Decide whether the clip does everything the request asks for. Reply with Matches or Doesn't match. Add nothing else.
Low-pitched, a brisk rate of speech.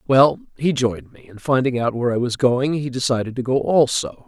Matches